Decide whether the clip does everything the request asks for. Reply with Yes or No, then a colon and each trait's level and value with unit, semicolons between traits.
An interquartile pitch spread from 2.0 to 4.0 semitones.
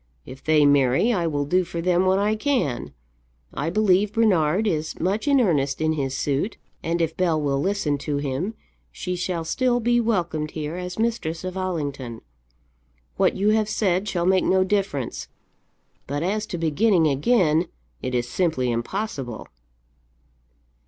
No: wide, 5.5 semitones